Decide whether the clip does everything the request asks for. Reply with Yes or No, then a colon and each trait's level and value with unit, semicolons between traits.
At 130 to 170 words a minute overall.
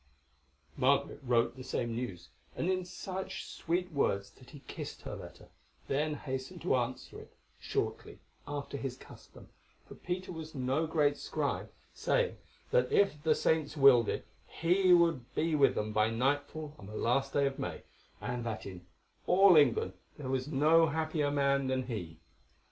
Yes: average, 165 wpm